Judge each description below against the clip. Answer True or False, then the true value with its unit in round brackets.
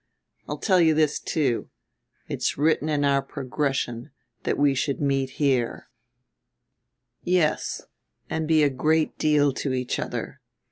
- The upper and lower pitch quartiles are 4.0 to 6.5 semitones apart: False (2.5 semitones)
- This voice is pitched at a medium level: True (145 Hz)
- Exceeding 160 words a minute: False (135 wpm)